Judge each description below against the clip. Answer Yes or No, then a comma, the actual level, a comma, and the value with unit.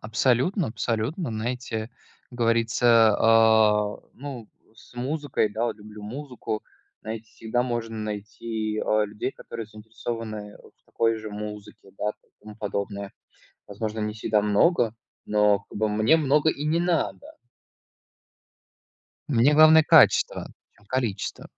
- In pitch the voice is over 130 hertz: No, low, 110 Hz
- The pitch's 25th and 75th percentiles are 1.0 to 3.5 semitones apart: Yes, narrow, 2.5 semitones